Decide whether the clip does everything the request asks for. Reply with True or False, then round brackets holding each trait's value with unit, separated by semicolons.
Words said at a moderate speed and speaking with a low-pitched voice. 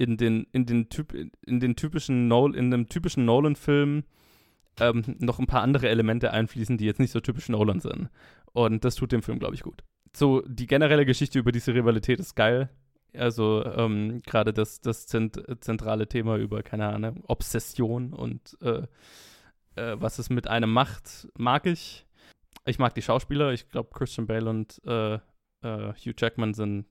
True (175 wpm; 120 Hz)